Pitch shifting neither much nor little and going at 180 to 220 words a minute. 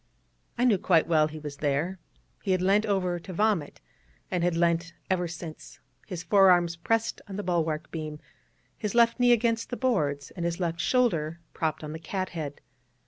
Yes: average, 4.1 semitones; average, 185 wpm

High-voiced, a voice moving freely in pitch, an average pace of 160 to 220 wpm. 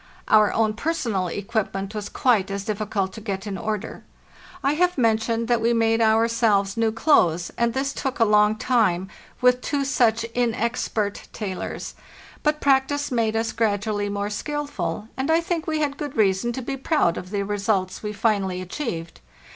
No: high, 220 Hz; average, 3.8 semitones; average, 170 wpm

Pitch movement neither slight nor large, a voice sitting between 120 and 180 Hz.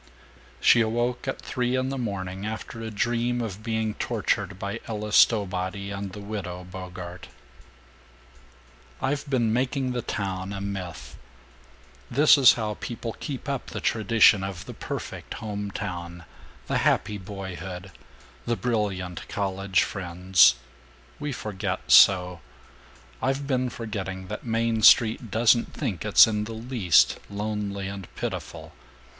No: average, 3.6 semitones; low, 105 Hz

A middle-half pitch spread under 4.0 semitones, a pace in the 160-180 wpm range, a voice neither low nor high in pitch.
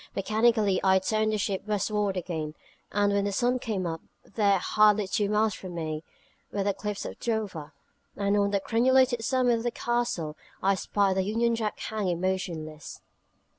No: narrow, 2.6 semitones; average, 170 wpm; high, 205 Hz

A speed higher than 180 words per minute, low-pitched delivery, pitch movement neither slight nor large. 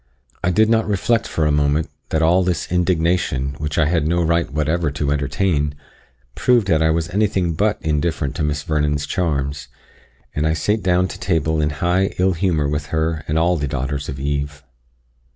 Yes: average, 190 wpm; very low, 80 Hz; average, 3.3 semitones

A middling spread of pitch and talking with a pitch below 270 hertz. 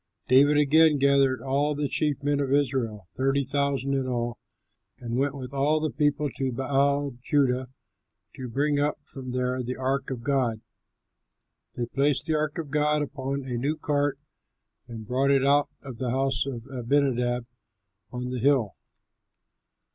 No: narrow, 2.1 semitones; low, 135 Hz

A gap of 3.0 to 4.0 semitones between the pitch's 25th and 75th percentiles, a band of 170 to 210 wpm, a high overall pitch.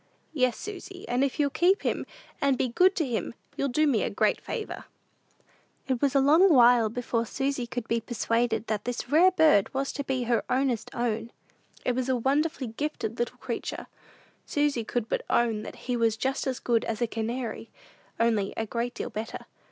Yes: average, 3.4 semitones; average, 190 wpm; high, 245 Hz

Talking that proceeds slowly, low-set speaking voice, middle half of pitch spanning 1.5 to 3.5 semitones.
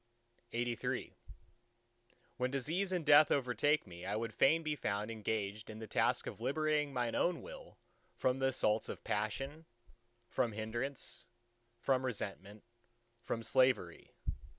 No: slow, 130 wpm; low, 125 Hz; average, 5.0 semitones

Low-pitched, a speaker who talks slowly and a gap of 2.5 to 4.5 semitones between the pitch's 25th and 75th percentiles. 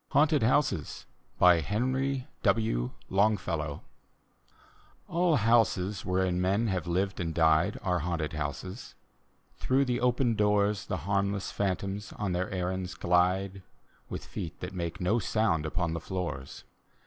Yes: very low, 95 Hz; slow, 125 wpm; average, 3.6 semitones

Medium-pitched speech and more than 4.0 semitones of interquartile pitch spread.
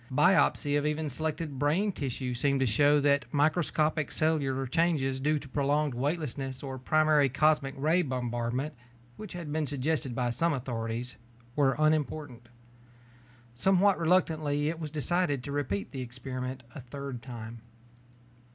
No: medium, 145 Hz; average, 3.2 semitones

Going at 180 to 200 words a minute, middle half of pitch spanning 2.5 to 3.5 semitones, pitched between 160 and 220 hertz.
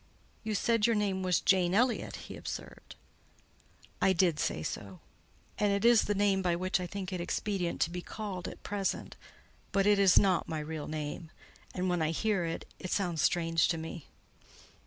Yes: average, 185 wpm; average, 3.2 semitones; medium, 185 Hz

